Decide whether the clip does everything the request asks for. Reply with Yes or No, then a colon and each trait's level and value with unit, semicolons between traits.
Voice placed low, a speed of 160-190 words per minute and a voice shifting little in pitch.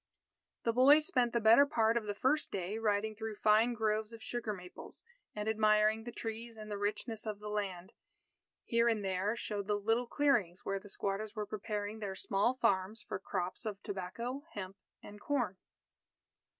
No: high, 215 Hz; average, 175 wpm; narrow, 2.3 semitones